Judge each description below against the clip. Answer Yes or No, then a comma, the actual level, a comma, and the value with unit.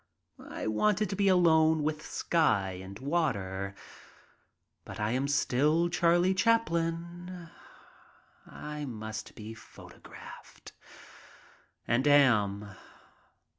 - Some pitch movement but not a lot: No, wide, 7.9 semitones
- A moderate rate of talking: No, slow, 95 wpm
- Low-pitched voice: No, medium, 150 Hz